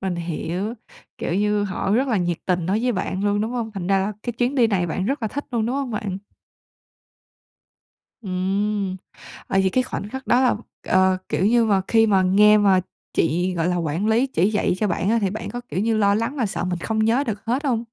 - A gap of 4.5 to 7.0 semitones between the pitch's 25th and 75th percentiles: No, average, 3.5 semitones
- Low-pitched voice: No, high, 205 Hz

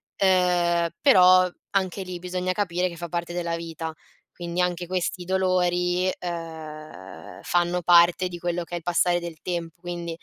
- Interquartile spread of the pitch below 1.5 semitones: Yes, narrow, 1.1 semitones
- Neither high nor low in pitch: Yes, medium, 175 Hz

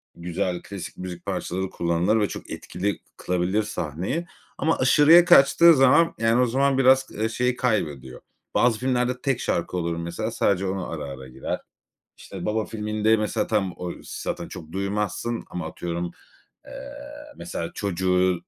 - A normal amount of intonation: No, wide, 5.9 semitones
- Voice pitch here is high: No, low, 100 Hz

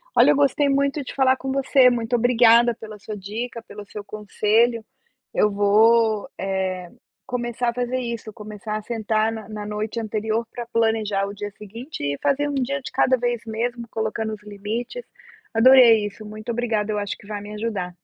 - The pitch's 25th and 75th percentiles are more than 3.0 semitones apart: No, narrow, 2.6 semitones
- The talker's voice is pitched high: Yes, high, 225 Hz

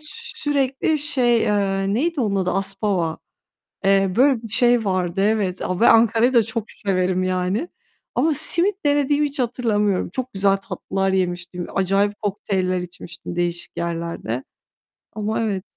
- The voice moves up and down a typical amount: Yes, average, 4.7 semitones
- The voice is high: Yes, high, 200 Hz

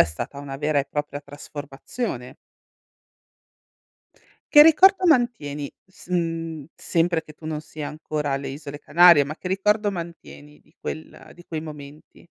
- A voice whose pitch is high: No, medium, 155 Hz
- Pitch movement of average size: Yes, average, 3.4 semitones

